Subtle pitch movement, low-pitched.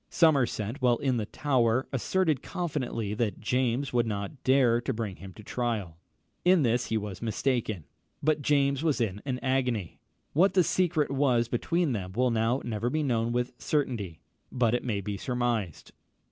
No: average, 3.8 semitones; low, 120 Hz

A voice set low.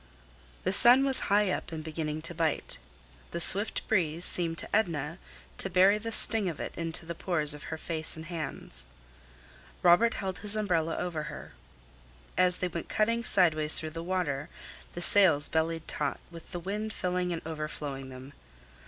No: medium, 170 Hz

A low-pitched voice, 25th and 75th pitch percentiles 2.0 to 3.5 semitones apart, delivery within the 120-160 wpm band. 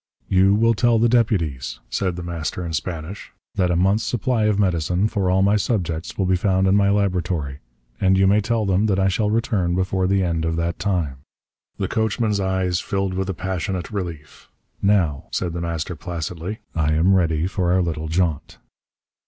No: very low, 95 Hz; average, 2.9 semitones; average, 190 wpm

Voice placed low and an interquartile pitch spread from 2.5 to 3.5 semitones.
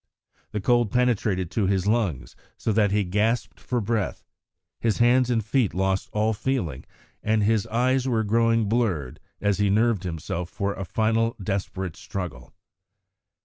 Yes: low, 105 Hz; average, 3.2 semitones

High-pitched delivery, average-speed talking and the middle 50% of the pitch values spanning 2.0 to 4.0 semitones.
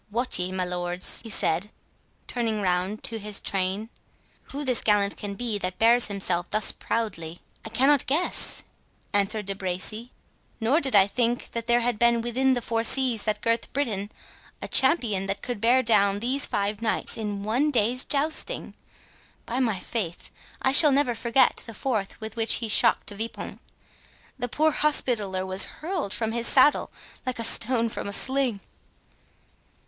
Yes: high, 225 Hz; average, 165 wpm; average, 3.7 semitones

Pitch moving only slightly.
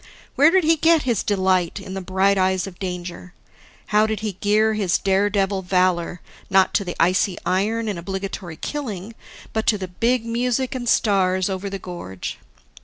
No: average, 3.0 semitones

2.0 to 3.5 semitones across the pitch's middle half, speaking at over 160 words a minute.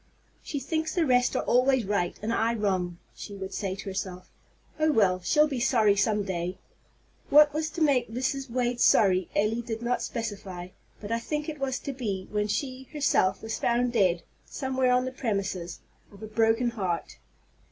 No: average, 4.8 semitones; average, 185 wpm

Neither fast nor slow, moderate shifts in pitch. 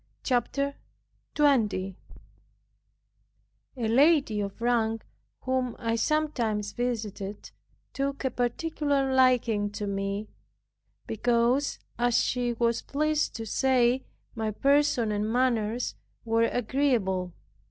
No: slow, 100 wpm; average, 3.5 semitones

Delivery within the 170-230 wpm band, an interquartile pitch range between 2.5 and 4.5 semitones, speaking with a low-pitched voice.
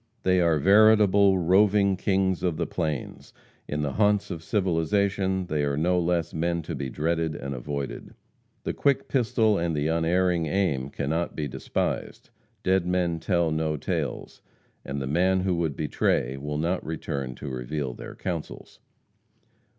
No: average, 155 wpm; average, 4.1 semitones; very low, 85 Hz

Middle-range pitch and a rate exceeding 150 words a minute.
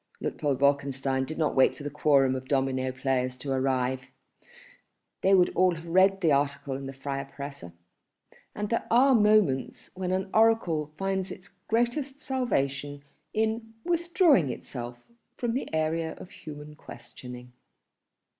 No: medium, 150 Hz; average, 145 wpm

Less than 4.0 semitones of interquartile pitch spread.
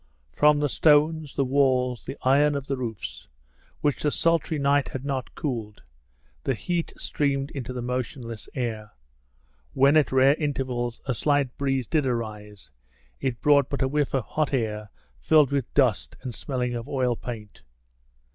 Yes: average, 2.9 semitones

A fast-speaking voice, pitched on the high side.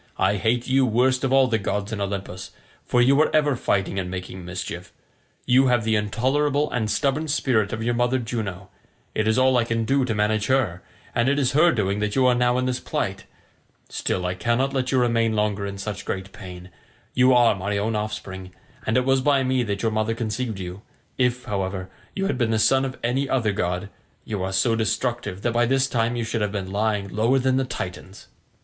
No: fast, 220 wpm; low, 115 Hz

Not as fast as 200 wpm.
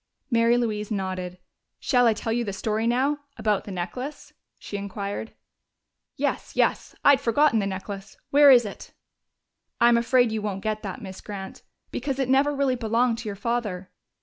Yes: average, 175 wpm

